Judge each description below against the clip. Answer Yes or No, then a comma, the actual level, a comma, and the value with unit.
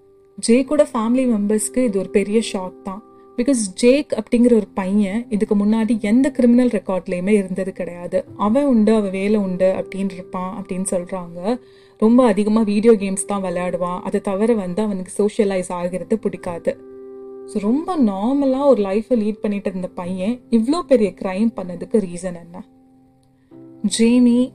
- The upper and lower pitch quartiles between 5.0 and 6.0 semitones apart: No, average, 4.0 semitones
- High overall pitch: Yes, high, 205 Hz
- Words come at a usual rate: No, fast, 140 wpm